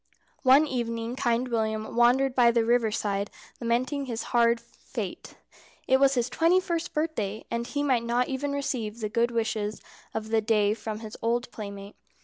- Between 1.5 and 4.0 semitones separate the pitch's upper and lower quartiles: Yes, average, 2.8 semitones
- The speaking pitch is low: No, high, 235 Hz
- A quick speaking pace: No, average, 170 wpm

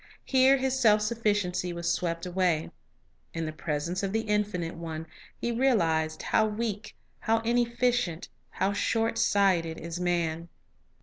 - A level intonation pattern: No, average, 5.1 semitones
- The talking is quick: No, average, 140 wpm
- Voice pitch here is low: No, high, 195 Hz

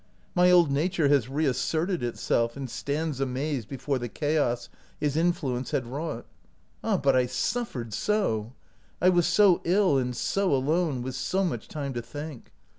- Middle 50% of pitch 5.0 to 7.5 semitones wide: Yes, wide, 5.4 semitones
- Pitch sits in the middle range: Yes, medium, 145 Hz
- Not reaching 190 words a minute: Yes, average, 165 wpm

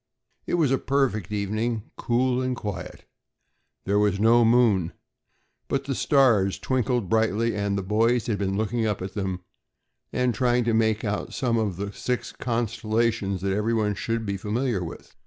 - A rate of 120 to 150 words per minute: No, average, 165 wpm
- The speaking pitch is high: No, low, 110 Hz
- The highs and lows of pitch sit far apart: No, average, 3.1 semitones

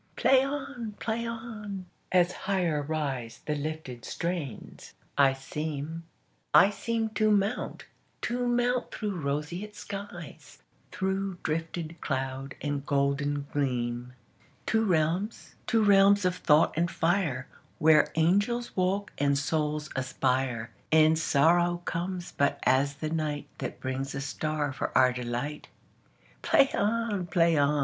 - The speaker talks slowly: Yes, slow, 110 wpm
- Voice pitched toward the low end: No, medium, 160 Hz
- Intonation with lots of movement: Yes, wide, 5.9 semitones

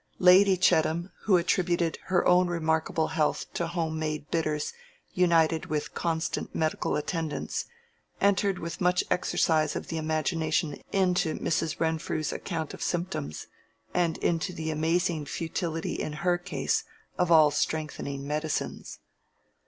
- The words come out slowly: Yes, slow, 130 wpm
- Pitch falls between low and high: Yes, medium, 165 Hz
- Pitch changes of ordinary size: No, narrow, 2.1 semitones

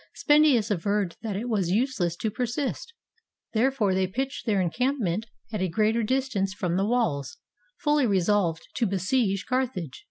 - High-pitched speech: Yes, high, 215 Hz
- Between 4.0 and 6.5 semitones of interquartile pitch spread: Yes, average, 5.1 semitones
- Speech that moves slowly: No, average, 160 wpm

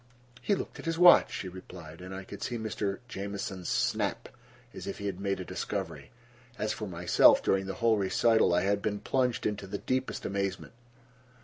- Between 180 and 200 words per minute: Yes, average, 190 wpm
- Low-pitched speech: Yes, low, 100 Hz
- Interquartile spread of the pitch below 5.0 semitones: Yes, average, 2.8 semitones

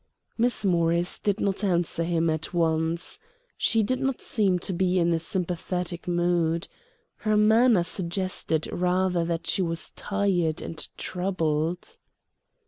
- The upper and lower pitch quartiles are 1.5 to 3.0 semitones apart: Yes, narrow, 2.6 semitones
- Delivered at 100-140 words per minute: Yes, slow, 135 wpm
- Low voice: No, medium, 175 Hz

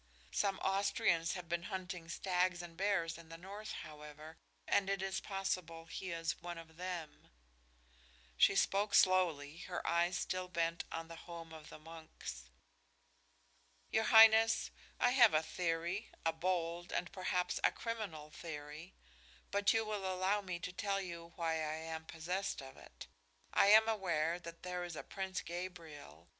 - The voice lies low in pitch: No, medium, 175 Hz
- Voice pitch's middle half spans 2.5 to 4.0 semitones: Yes, average, 2.8 semitones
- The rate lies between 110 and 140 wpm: No, average, 160 wpm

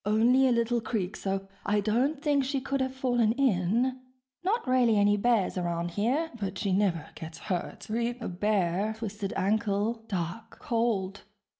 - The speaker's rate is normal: Yes, average, 160 wpm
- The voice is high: Yes, high, 220 Hz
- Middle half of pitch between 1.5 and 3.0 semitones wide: No, average, 4.0 semitones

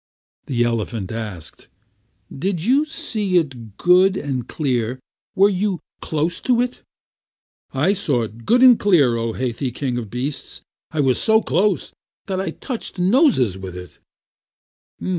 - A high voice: No, medium, 145 Hz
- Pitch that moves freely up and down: Yes, wide, 8.8 semitones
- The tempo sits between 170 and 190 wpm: No, average, 140 wpm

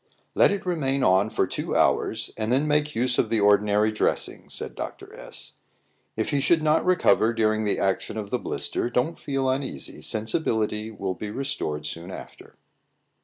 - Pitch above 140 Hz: No, low, 110 Hz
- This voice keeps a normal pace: Yes, average, 170 wpm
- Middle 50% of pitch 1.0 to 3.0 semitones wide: No, average, 4.7 semitones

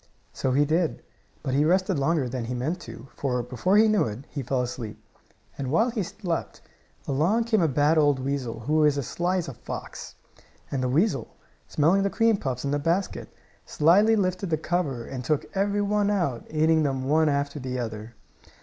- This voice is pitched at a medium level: Yes, medium, 150 Hz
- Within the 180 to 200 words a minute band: Yes, average, 195 wpm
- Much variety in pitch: Yes, wide, 5.7 semitones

